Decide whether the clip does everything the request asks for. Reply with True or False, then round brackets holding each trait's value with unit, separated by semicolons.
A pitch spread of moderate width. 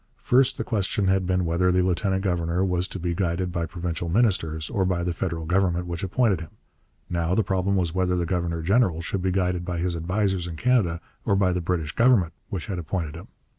False (2.1 semitones)